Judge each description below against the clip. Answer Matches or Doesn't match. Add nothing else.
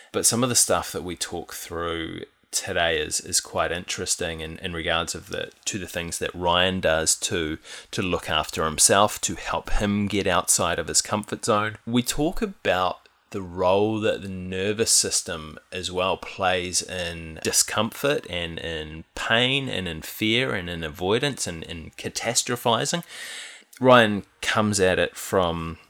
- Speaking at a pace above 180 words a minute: Doesn't match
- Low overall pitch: Matches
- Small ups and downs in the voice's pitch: Doesn't match